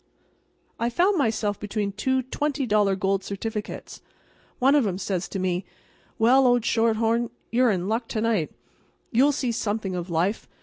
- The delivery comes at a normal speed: Yes, average, 155 wpm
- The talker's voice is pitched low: No, high, 220 Hz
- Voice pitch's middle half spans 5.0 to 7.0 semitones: No, average, 3.7 semitones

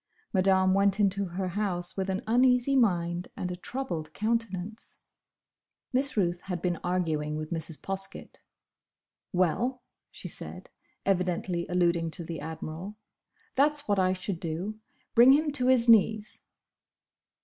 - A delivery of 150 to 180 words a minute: No, slow, 135 wpm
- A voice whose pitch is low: No, high, 190 Hz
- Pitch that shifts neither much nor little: Yes, average, 4.2 semitones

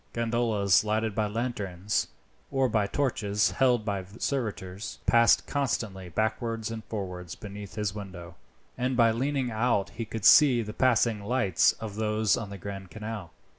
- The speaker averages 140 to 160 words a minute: Yes, average, 150 wpm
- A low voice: Yes, low, 110 Hz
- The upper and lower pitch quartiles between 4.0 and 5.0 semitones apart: No, average, 2.7 semitones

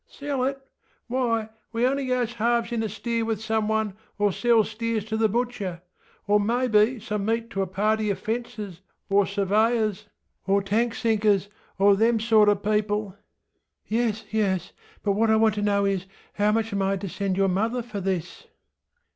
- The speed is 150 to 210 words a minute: Yes, average, 170 wpm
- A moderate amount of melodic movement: No, narrow, 2.3 semitones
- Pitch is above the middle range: Yes, high, 215 Hz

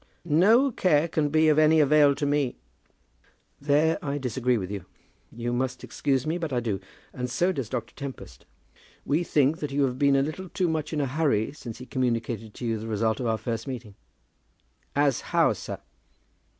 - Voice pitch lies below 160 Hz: Yes, low, 135 Hz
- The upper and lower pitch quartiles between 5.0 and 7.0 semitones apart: No, average, 4.2 semitones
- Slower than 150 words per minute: No, average, 190 wpm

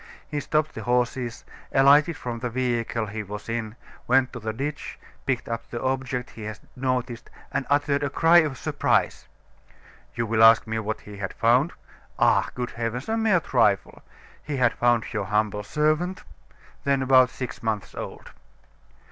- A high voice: No, low, 125 Hz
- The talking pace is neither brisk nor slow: Yes, average, 165 wpm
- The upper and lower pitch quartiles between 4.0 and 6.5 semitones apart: No, average, 3.5 semitones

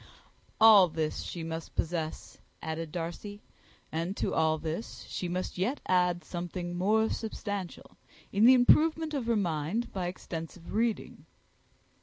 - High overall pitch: No, medium, 180 Hz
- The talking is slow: Yes, slow, 130 wpm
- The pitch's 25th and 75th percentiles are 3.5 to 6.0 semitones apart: Yes, average, 4.8 semitones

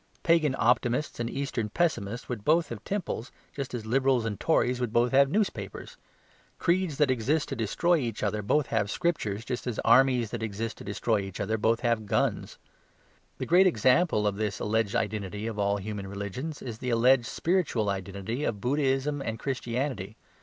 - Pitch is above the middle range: No, low, 120 Hz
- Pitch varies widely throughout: No, average, 4.6 semitones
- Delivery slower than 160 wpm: No, average, 175 wpm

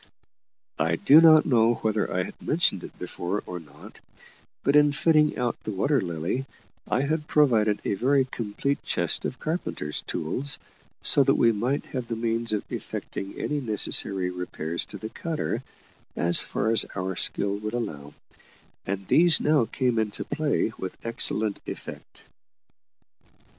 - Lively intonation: Yes, wide, 6.4 semitones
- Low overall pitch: Yes, low, 115 Hz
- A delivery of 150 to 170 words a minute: Yes, average, 155 wpm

